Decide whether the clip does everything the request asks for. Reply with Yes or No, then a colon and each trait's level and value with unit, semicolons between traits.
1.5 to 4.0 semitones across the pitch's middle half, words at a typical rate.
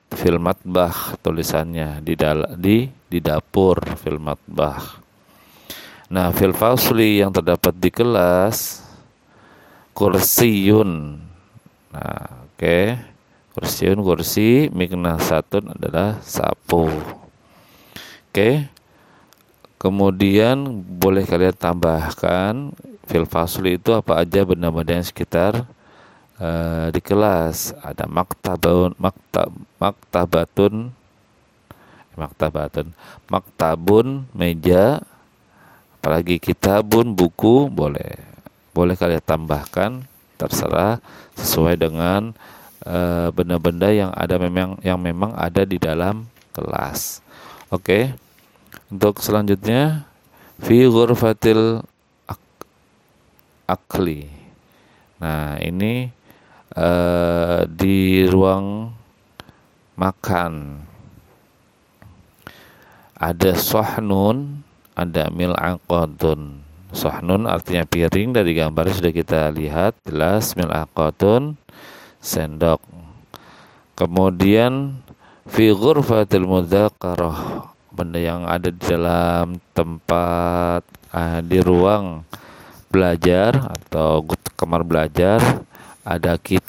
No: average, 3.6 semitones; slow, 80 wpm